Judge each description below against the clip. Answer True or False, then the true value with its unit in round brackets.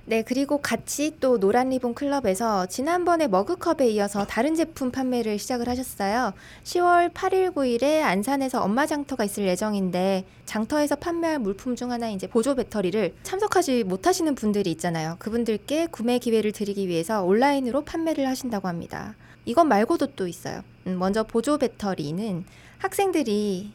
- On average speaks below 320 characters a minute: False (365 characters per minute)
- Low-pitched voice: False (240 Hz)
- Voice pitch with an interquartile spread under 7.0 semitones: True (6.3 semitones)